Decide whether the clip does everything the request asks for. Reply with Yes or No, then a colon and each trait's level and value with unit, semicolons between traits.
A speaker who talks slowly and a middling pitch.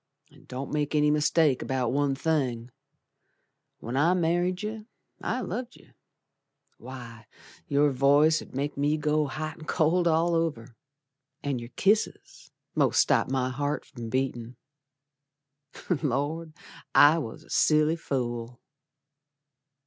Yes: slow, 125 wpm; medium, 145 Hz